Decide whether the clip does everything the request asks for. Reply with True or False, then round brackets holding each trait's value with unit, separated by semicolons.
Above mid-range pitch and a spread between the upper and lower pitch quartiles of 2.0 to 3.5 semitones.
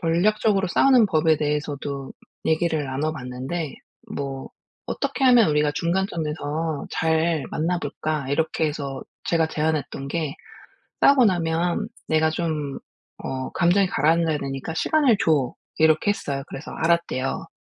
False (160 Hz; 3.0 semitones)